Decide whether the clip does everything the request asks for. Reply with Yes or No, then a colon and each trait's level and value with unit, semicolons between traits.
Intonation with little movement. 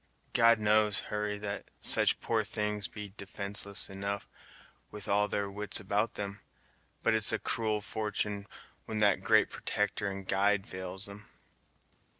Yes: narrow, 1.0 semitones